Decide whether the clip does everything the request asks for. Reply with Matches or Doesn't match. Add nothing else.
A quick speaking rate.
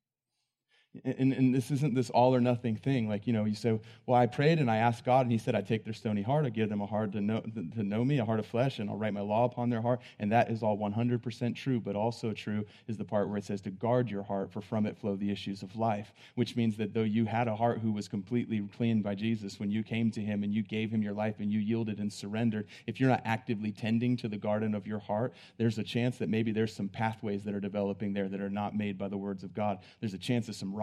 Matches